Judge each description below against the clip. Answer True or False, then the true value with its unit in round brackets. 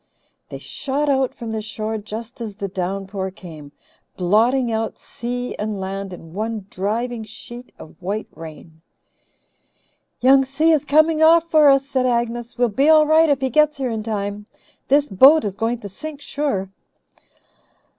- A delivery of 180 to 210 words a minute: False (165 wpm)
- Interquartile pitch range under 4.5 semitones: False (5.4 semitones)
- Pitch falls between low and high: False (235 Hz)